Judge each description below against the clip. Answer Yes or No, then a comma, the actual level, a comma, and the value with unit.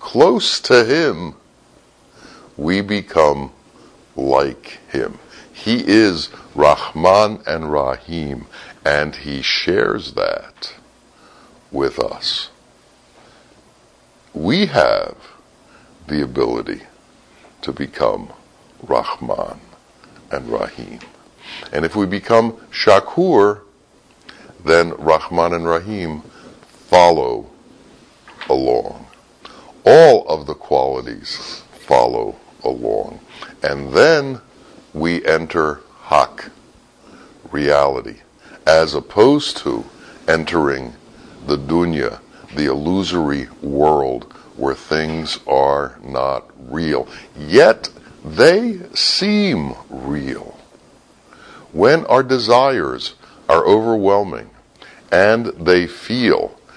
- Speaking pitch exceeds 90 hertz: No, very low, 85 Hz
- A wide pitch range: Yes, wide, 6.2 semitones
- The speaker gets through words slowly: Yes, slow, 80 wpm